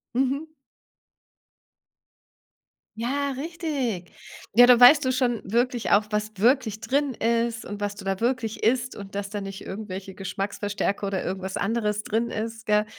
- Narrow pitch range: No, average, 3.6 semitones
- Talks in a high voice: Yes, high, 220 Hz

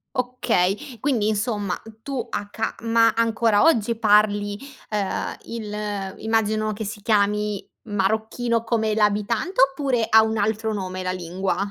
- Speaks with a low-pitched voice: No, high, 215 Hz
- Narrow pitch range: Yes, narrow, 2.0 semitones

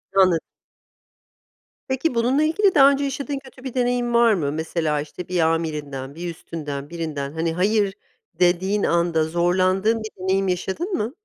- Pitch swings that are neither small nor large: No, wide, 6.8 semitones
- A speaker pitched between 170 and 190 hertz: Yes, medium, 185 Hz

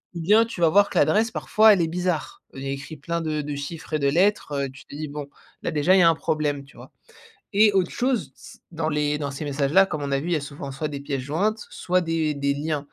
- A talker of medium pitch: Yes, medium, 155 Hz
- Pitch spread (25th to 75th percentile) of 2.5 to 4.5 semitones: Yes, average, 4.0 semitones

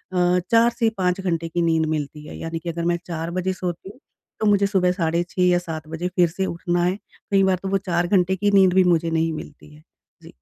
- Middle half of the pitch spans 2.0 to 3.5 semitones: Yes, narrow, 2.4 semitones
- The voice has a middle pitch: Yes, medium, 175 Hz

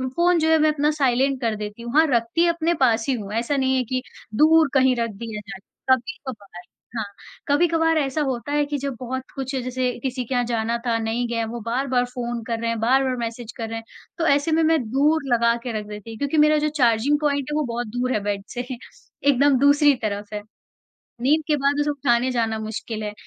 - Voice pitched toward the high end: Yes, very high, 255 Hz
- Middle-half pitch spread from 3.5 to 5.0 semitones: Yes, average, 3.8 semitones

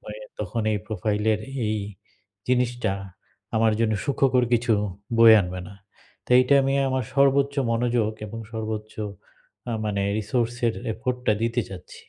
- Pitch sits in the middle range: No, low, 115 Hz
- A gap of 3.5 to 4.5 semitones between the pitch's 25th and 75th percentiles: No, average, 2.7 semitones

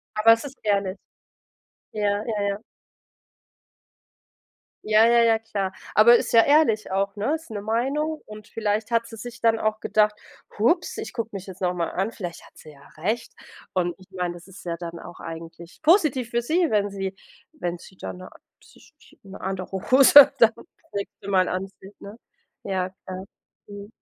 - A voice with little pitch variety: No, average, 3.5 semitones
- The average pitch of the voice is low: No, high, 210 Hz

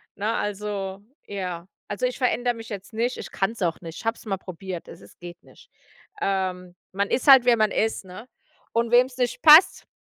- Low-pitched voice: No, high, 205 Hz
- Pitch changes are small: No, average, 4.2 semitones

